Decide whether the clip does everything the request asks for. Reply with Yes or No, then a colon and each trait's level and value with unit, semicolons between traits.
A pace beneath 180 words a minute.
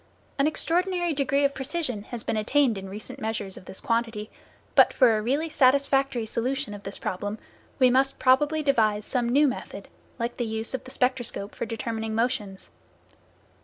Yes: average, 170 wpm